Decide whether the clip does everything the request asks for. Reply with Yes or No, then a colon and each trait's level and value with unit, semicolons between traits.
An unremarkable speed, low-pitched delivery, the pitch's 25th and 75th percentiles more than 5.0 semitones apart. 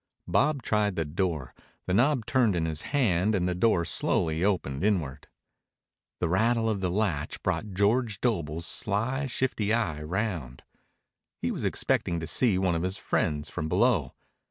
Yes: average, 160 wpm; very low, 95 Hz; wide, 5.4 semitones